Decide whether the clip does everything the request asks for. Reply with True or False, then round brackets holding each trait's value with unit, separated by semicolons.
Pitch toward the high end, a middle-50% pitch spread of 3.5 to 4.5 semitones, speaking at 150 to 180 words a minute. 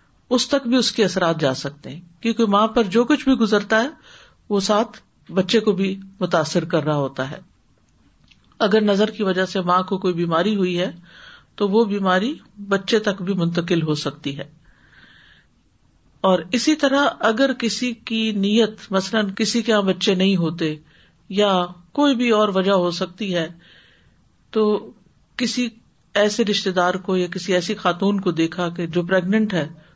True (195 Hz; 4.0 semitones; 170 wpm)